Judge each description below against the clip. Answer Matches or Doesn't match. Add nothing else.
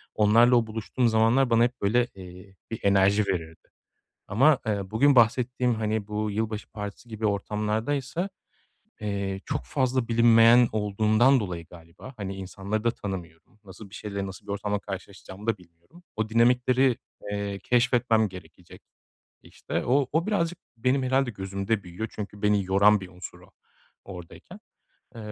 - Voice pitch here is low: Matches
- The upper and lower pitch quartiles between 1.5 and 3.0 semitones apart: Doesn't match